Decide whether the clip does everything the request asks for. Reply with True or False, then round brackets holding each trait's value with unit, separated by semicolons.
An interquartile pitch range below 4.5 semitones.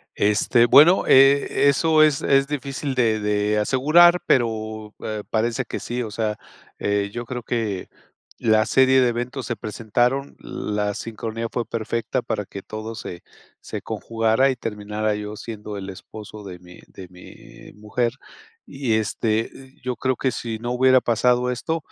True (3.4 semitones)